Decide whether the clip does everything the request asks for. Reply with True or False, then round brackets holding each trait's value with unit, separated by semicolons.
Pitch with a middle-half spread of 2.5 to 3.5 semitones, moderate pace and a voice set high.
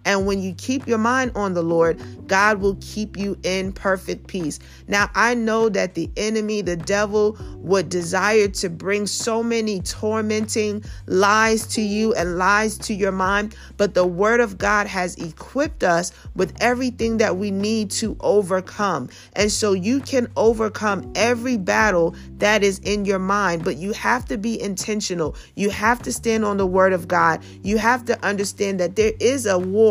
True (2.8 semitones; 180 wpm; 205 Hz)